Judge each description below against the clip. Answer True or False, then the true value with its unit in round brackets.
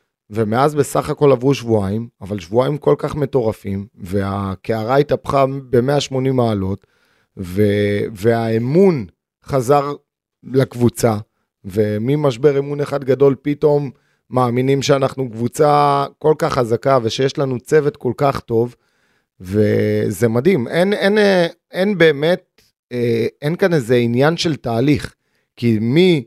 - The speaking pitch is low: True (130 Hz)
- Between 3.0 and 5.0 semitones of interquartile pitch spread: True (4.3 semitones)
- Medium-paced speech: True (110 wpm)